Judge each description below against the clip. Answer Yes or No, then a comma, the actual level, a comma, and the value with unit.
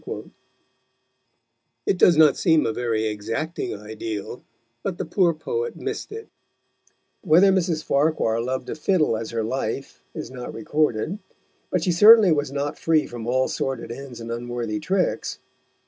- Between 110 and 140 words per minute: No, average, 150 wpm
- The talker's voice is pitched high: No, medium, 140 Hz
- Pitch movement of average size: No, wide, 6.6 semitones